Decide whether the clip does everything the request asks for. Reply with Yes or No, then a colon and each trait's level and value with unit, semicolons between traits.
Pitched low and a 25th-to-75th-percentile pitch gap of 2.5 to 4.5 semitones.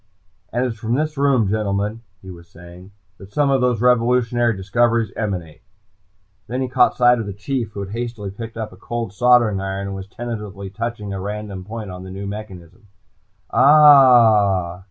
Yes: low, 110 Hz; average, 3.7 semitones